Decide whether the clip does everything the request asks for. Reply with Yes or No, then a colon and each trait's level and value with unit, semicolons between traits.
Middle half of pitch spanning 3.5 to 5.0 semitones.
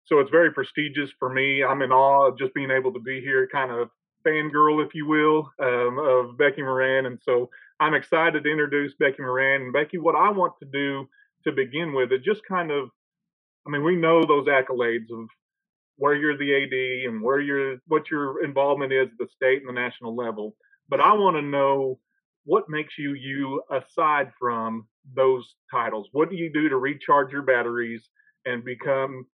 No: average, 2.8 semitones